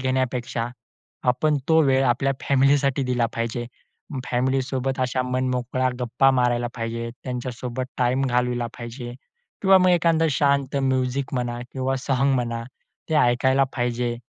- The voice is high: No, low, 130 Hz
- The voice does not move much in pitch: Yes, narrow, 1.9 semitones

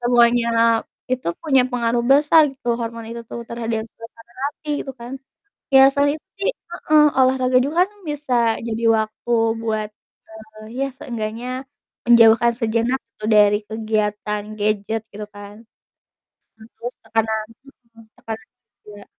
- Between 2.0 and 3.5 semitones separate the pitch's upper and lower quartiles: Yes, average, 2.7 semitones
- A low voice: No, high, 230 Hz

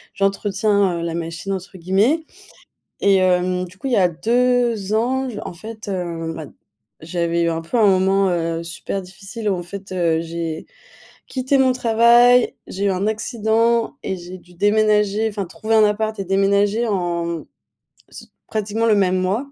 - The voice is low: No, high, 195 Hz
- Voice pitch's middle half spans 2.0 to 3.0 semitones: No, average, 3.7 semitones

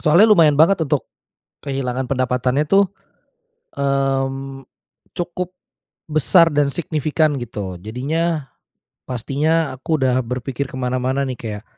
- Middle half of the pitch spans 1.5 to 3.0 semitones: No, average, 3.4 semitones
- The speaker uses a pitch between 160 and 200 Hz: No, low, 135 Hz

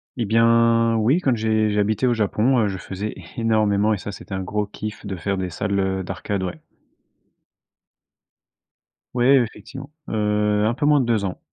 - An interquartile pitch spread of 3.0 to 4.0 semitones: No, narrow, 2.5 semitones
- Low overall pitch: Yes, low, 110 Hz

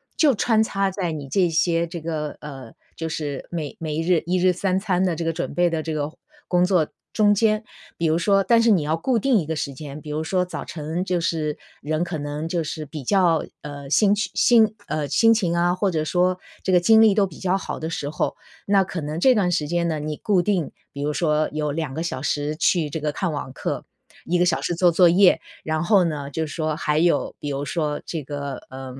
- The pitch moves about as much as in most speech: Yes, average, 3.4 semitones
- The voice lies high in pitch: No, medium, 165 Hz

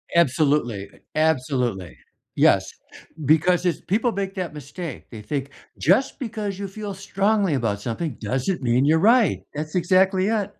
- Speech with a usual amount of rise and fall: No, wide, 6.6 semitones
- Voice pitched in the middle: Yes, medium, 165 Hz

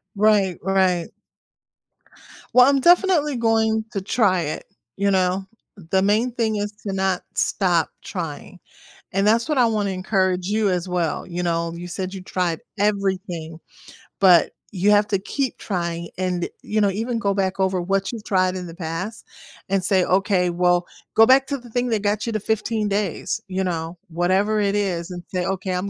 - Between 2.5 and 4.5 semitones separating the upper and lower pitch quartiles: Yes, average, 2.9 semitones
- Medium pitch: No, high, 195 Hz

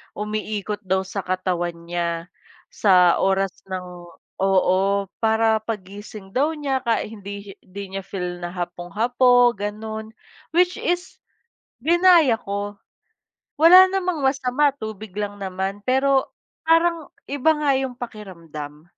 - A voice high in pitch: Yes, high, 210 Hz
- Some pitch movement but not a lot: No, wide, 5.9 semitones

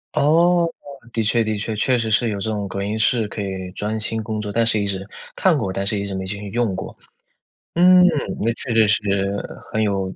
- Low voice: Yes, low, 110 Hz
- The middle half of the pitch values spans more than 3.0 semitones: No, narrow, 2.6 semitones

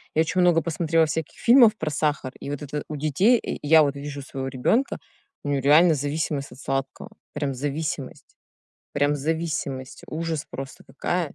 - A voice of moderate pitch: Yes, medium, 150 Hz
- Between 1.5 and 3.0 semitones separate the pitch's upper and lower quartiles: Yes, narrow, 2.6 semitones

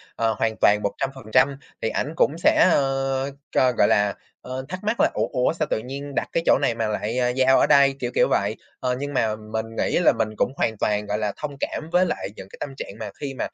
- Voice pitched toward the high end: No, low, 130 Hz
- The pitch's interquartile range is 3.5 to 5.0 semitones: Yes, average, 4.2 semitones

